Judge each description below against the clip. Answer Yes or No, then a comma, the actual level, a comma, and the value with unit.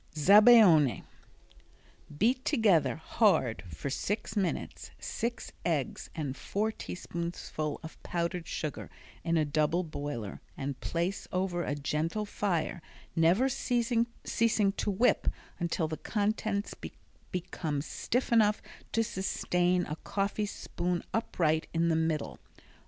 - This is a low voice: No, medium, 175 Hz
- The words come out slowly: Yes, slow, 115 wpm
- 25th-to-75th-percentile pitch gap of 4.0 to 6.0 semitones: Yes, average, 5.0 semitones